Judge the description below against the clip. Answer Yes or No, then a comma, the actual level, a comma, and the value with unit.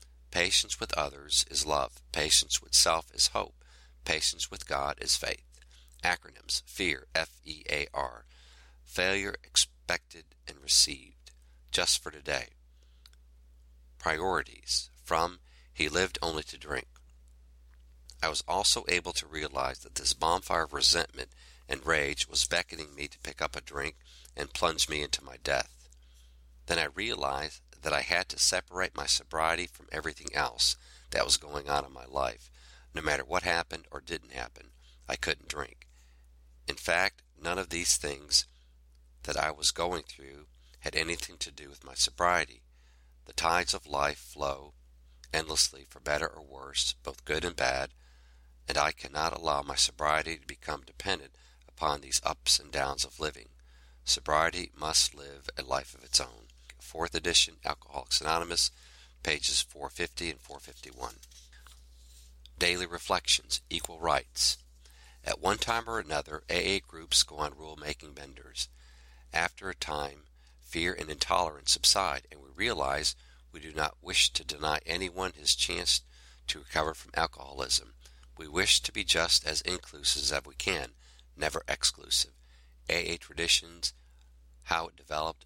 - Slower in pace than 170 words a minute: Yes, average, 145 wpm